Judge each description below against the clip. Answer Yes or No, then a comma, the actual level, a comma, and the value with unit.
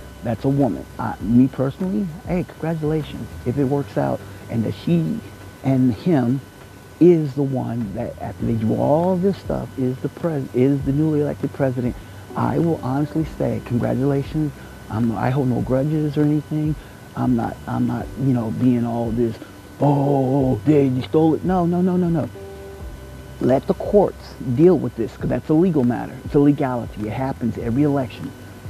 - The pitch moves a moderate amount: Yes, average, 4.4 semitones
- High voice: No, low, 130 Hz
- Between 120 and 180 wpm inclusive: Yes, average, 175 wpm